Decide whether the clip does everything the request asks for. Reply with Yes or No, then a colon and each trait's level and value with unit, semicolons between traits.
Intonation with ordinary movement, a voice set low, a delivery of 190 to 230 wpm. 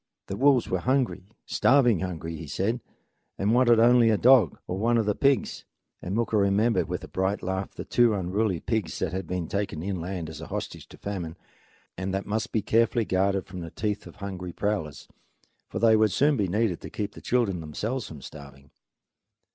Yes: average, 4.0 semitones; low, 100 Hz; average, 195 wpm